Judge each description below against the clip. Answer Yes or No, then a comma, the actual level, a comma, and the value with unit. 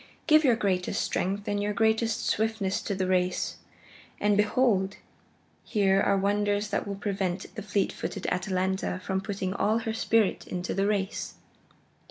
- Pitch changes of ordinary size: No, narrow, 2.0 semitones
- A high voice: Yes, high, 200 Hz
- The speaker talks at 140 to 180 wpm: Yes, average, 155 wpm